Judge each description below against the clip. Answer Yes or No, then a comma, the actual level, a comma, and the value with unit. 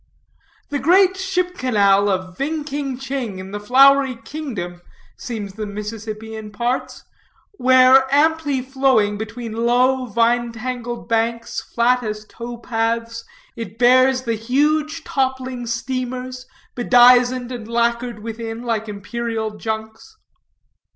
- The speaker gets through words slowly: Yes, slow, 120 wpm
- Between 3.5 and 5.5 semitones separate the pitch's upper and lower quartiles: No, average, 2.9 semitones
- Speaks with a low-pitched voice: No, high, 240 Hz